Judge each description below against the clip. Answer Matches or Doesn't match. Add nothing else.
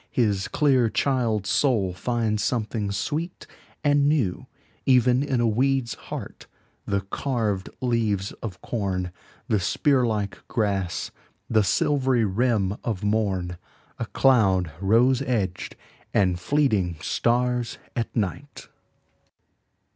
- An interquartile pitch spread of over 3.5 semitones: Matches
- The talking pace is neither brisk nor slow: Doesn't match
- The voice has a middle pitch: Doesn't match